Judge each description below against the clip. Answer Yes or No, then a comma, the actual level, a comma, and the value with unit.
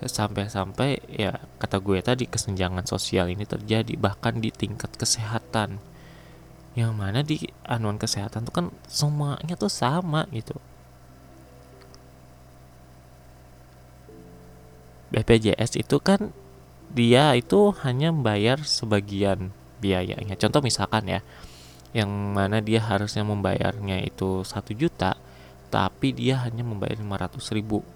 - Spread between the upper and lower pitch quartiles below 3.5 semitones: No, average, 5.1 semitones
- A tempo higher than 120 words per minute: No, average, 105 wpm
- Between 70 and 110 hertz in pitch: Yes, low, 105 Hz